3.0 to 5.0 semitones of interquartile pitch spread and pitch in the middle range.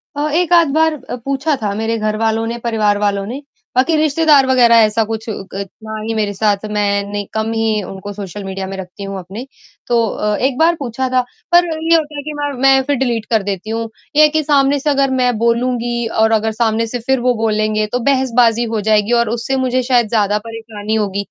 No: average, 4.0 semitones; high, 230 Hz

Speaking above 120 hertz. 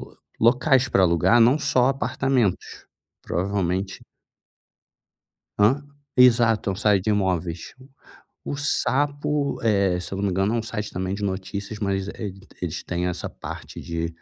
No: low, 100 Hz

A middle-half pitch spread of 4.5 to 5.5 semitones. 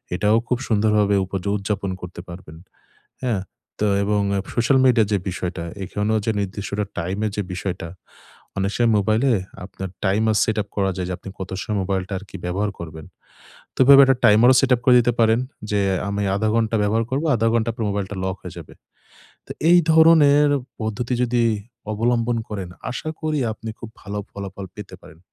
No: average, 3.2 semitones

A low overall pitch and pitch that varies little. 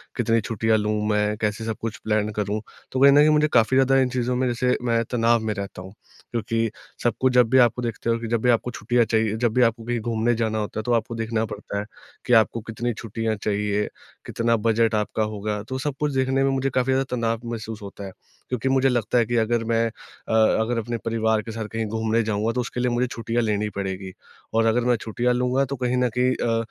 Yes: low, 115 Hz; narrow, 2.2 semitones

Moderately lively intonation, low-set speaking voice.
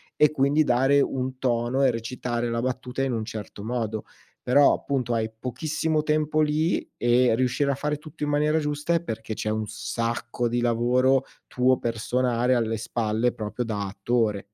Yes: average, 3.3 semitones; low, 125 Hz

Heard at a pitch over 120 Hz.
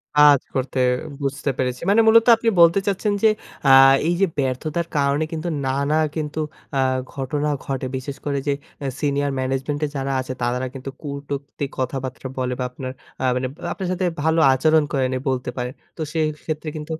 Yes: medium, 140 Hz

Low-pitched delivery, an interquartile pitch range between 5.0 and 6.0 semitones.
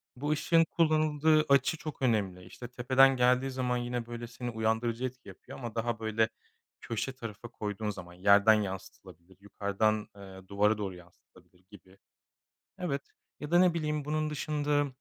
Yes: low, 120 Hz; wide, 5.4 semitones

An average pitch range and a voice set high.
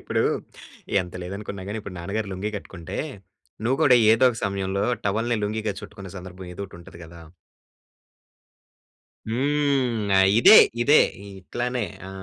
No: average, 4.1 semitones; low, 105 Hz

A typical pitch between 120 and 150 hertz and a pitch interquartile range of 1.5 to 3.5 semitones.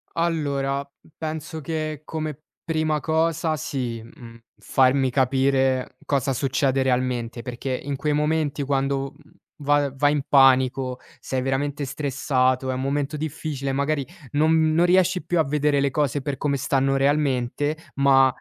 Yes: medium, 140 Hz; narrow, 2.4 semitones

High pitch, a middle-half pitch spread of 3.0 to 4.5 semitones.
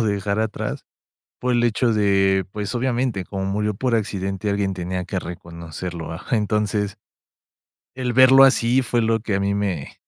No: low, 105 Hz; average, 3.3 semitones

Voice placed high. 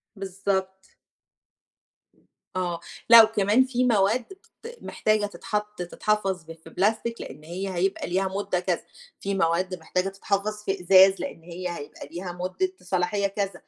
Yes: high, 195 Hz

